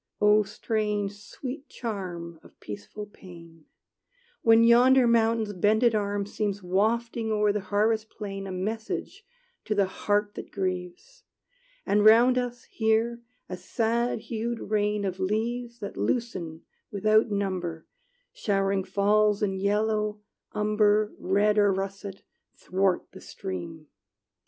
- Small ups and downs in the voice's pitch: Yes, narrow, 2.3 semitones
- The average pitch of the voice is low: No, high, 210 Hz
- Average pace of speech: No, slow, 125 wpm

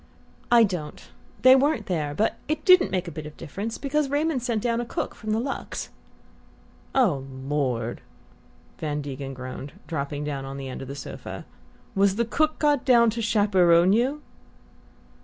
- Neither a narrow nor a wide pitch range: No, wide, 9.0 semitones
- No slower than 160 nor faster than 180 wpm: Yes, average, 170 wpm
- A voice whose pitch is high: Yes, high, 195 Hz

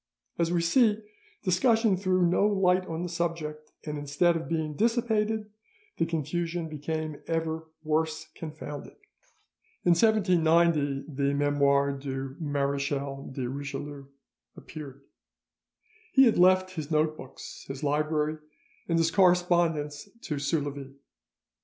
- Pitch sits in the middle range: Yes, medium, 160 Hz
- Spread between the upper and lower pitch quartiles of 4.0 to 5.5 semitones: No, average, 3.6 semitones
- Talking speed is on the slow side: Yes, slow, 120 wpm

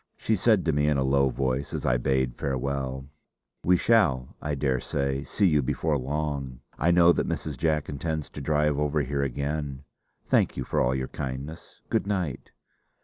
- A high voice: No, very low, 70 Hz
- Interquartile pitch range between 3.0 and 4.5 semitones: No, narrow, 2.6 semitones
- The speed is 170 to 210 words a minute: Yes, average, 180 wpm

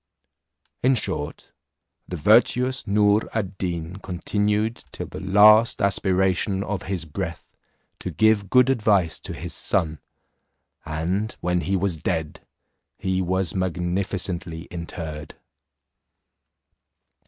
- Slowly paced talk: Yes, slow, 110 wpm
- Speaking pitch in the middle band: No, very low, 95 Hz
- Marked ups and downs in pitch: No, average, 3.2 semitones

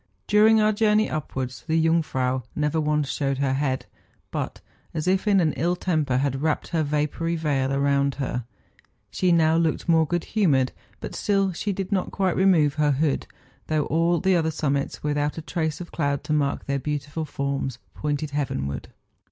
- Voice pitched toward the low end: No, medium, 150 Hz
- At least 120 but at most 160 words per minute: No, average, 175 wpm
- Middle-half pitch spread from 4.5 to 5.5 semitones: No, average, 3.5 semitones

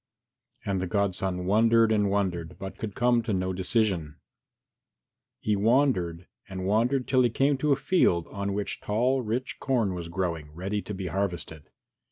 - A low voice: Yes, low, 100 Hz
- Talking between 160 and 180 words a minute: Yes, average, 165 wpm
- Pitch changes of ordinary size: Yes, average, 4.1 semitones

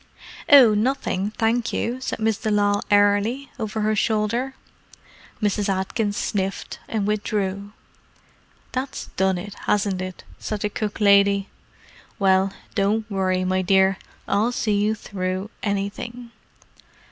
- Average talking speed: No, slow, 125 wpm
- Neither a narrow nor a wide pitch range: No, narrow, 2.1 semitones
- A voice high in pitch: Yes, high, 205 Hz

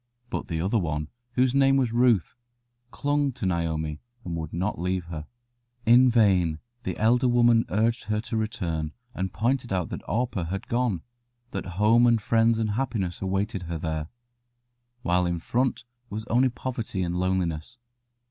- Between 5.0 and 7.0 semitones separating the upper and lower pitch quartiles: Yes, wide, 5.5 semitones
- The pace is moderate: Yes, average, 160 wpm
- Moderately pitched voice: No, low, 105 Hz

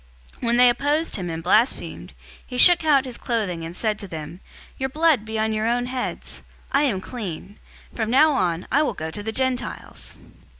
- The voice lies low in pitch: No, high, 235 Hz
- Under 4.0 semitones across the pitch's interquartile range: No, average, 5.2 semitones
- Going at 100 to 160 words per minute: No, average, 200 wpm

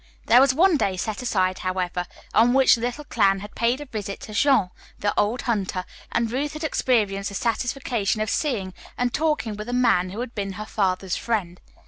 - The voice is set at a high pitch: Yes, high, 220 Hz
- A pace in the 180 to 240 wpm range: Yes, average, 200 wpm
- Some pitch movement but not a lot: Yes, average, 4.2 semitones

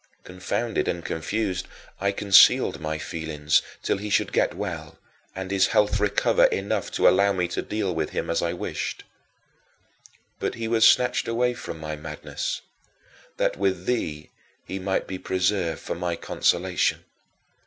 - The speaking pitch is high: No, very low, 95 Hz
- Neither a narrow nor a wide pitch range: Yes, average, 3.4 semitones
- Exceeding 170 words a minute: No, average, 155 wpm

